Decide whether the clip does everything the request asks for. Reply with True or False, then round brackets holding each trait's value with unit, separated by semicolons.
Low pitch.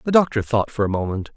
True (120 Hz)